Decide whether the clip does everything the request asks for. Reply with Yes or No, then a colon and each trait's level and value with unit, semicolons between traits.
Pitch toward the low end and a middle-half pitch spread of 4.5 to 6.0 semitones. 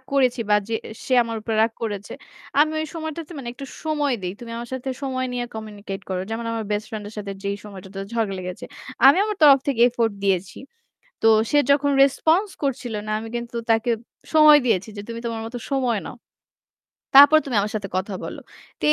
No: high, 235 Hz; average, 4.8 semitones